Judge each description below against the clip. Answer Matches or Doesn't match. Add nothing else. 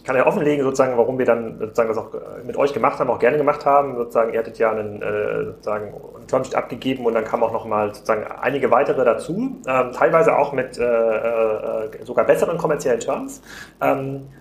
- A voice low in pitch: Matches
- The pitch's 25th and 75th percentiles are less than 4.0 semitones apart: Doesn't match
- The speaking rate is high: Matches